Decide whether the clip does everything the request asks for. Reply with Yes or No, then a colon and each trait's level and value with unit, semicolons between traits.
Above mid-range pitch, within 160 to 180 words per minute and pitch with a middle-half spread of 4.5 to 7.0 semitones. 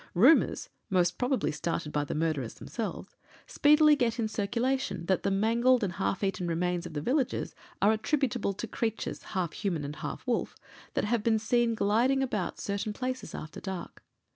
Yes: high, 210 Hz; average, 170 wpm; wide, 5.6 semitones